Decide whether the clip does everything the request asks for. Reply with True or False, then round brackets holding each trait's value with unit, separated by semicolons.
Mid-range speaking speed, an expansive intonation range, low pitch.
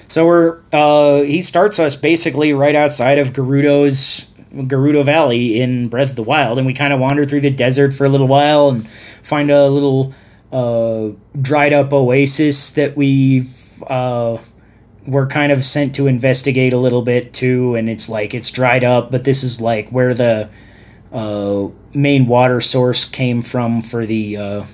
False (170 wpm; 3.4 semitones; 130 Hz)